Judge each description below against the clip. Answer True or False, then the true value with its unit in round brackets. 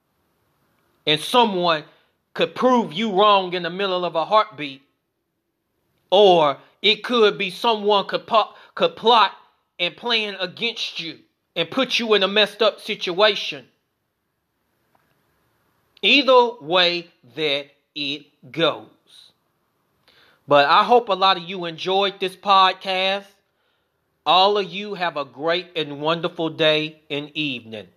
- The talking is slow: True (125 wpm)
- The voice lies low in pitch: False (185 Hz)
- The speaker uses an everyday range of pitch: True (4.5 semitones)